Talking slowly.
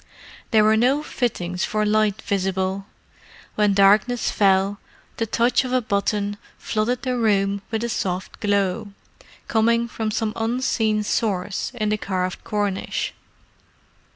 Yes: slow, 130 wpm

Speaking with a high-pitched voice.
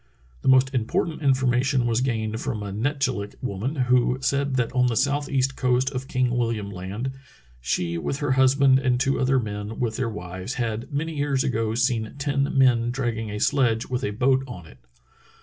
No: low, 125 Hz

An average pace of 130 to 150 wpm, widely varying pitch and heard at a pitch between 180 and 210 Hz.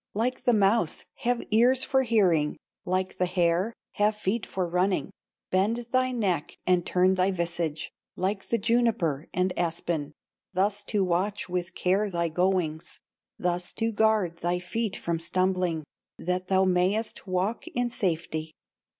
No: average, 145 wpm; average, 3.6 semitones; medium, 185 Hz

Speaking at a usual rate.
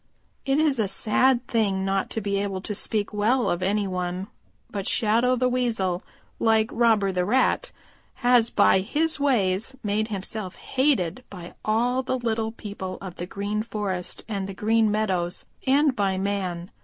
Yes: average, 165 wpm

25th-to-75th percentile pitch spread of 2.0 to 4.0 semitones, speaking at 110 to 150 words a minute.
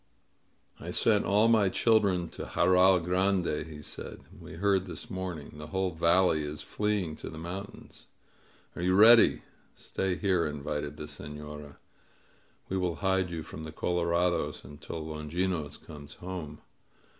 Yes: average, 3.7 semitones; average, 145 wpm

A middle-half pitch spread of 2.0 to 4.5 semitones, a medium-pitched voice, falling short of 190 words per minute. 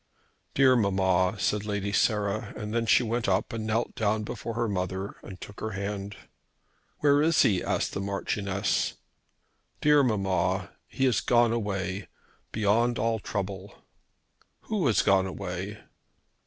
No: average, 2.9 semitones; low, 105 Hz; average, 140 wpm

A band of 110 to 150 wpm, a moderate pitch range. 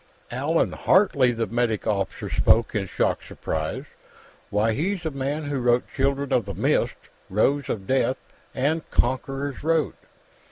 Yes: average, 145 wpm; average, 4.0 semitones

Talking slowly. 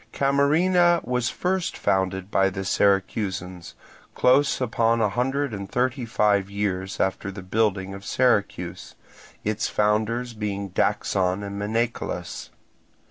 Yes: slow, 120 wpm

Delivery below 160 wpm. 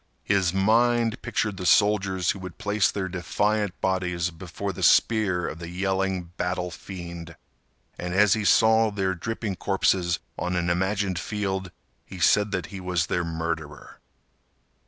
Yes: average, 150 wpm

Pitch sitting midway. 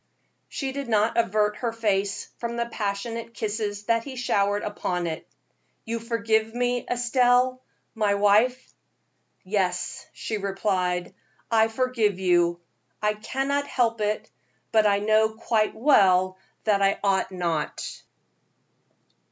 No: high, 215 Hz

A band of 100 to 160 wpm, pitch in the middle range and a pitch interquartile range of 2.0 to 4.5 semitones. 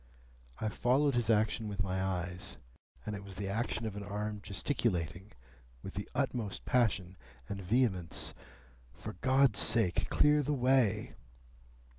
No: average, 140 wpm; low, 105 Hz; average, 4.1 semitones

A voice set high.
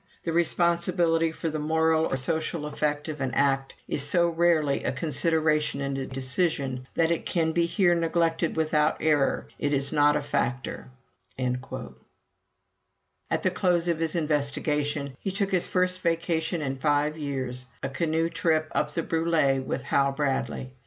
No: medium, 155 Hz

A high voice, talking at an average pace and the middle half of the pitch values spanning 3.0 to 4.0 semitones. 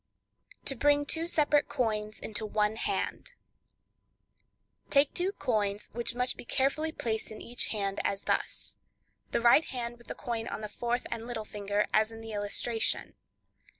Yes: high, 235 Hz; average, 155 wpm; average, 3.6 semitones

